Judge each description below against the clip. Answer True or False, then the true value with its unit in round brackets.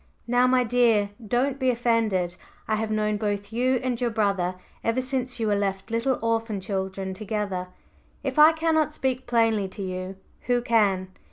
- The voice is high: True (225 Hz)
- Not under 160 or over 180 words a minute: True (170 wpm)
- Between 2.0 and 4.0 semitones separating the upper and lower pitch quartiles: True (3.7 semitones)